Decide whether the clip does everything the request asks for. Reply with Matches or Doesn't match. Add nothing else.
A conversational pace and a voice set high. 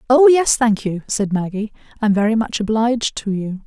Matches